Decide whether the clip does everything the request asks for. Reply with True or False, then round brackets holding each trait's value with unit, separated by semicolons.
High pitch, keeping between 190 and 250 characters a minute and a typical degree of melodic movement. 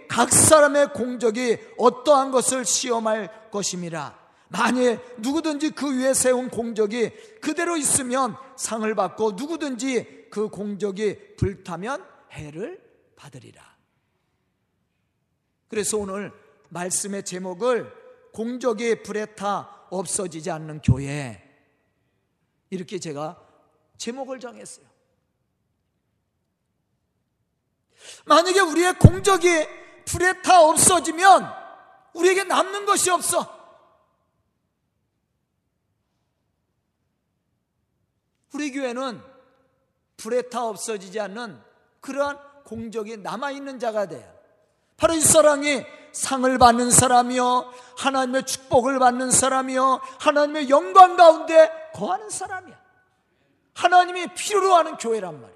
False (255 Hz; 225 characters per minute; 6.5 semitones)